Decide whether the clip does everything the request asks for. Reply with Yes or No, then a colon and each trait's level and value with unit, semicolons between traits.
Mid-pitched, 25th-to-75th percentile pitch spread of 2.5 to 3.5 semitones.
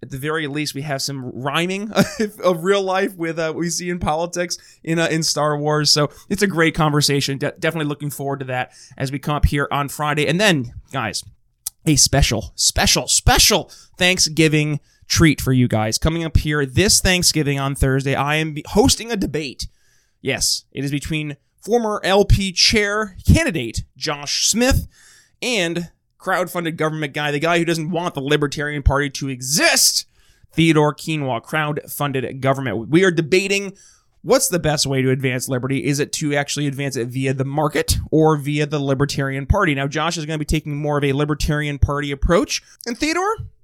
Yes: medium, 150 Hz; average, 3.2 semitones